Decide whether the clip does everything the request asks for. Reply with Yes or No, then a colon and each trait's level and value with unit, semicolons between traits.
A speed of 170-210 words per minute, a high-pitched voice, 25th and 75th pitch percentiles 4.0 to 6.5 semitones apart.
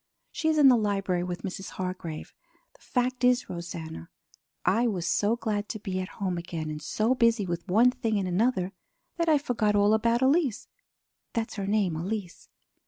Yes: average, 180 wpm; high, 205 Hz; average, 5.0 semitones